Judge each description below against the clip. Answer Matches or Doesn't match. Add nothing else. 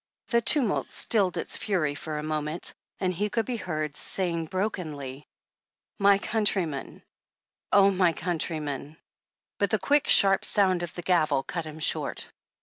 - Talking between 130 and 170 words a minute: Matches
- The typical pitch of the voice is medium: Matches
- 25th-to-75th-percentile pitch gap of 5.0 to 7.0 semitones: Doesn't match